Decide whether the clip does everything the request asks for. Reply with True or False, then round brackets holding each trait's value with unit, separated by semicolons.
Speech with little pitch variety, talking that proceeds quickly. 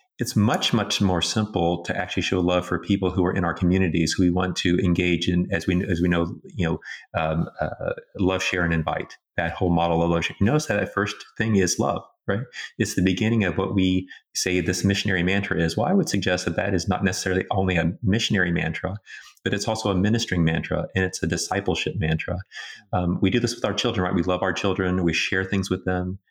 True (1.9 semitones; 230 wpm)